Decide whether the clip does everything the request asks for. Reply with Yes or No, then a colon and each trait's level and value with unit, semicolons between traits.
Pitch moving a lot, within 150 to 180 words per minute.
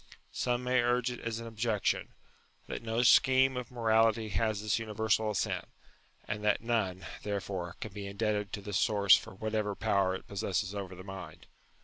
No: narrow, 2.5 semitones; average, 170 wpm